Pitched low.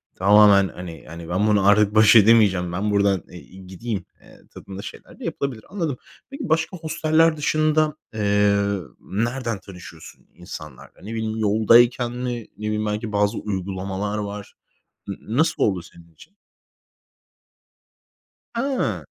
Yes: low, 105 Hz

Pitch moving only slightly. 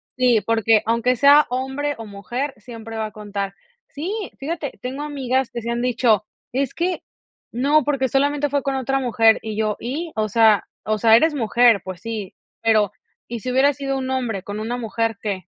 No: average, 3.7 semitones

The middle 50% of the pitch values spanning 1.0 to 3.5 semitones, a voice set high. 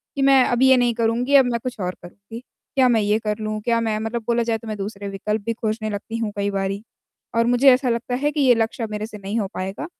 Yes: narrow, 2.6 semitones; high, 225 Hz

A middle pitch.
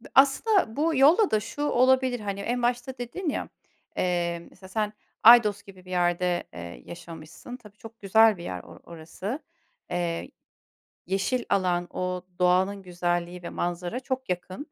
No: high, 195 Hz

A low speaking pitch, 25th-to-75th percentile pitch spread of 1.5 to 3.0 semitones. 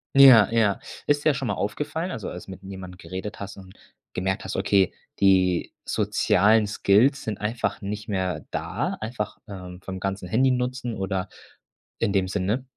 No: low, 100 Hz; average, 3.5 semitones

